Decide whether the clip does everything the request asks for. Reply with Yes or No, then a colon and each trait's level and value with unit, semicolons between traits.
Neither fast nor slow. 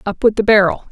No: fast, 265 wpm